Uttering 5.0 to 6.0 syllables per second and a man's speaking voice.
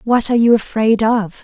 No: 5.3 syllables/s; female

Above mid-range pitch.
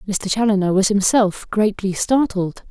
Yes: high, 205 Hz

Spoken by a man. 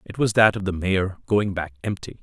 Yes: male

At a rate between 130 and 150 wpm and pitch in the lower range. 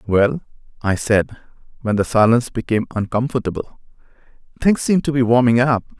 Yes: average, 140 wpm; low, 120 Hz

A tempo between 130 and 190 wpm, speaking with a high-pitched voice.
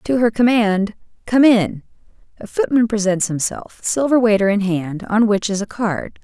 Yes: average, 175 wpm; high, 210 Hz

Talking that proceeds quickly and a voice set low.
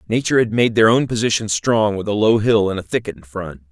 Yes: fast, 260 wpm; low, 105 Hz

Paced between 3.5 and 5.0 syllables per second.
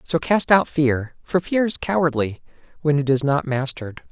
Yes: 4.9 syllables/s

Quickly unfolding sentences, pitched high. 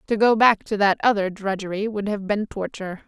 Yes: fast, 215 wpm; high, 205 Hz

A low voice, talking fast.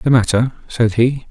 No: low, 120 Hz; average, 185 wpm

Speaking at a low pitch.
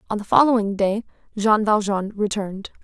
No: high, 210 Hz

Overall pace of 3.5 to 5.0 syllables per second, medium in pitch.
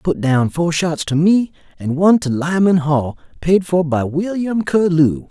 Yes: 4.2 syllables/s; medium, 165 Hz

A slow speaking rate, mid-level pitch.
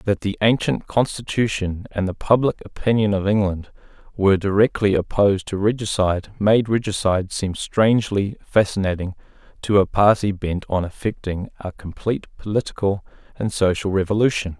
No: slow, 130 wpm; low, 100 Hz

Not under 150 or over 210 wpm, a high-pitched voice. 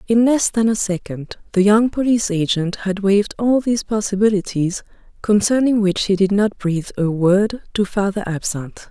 Yes: average, 170 wpm; high, 200 Hz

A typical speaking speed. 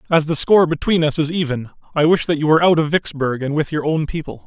No: fast, 270 wpm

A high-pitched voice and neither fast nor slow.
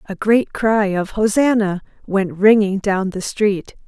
Yes: high, 205 Hz; average, 155 wpm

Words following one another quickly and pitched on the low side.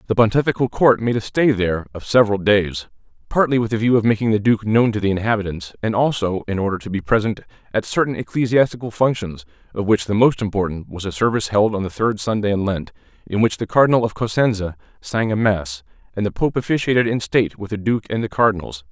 Yes: fast, 220 wpm; low, 105 Hz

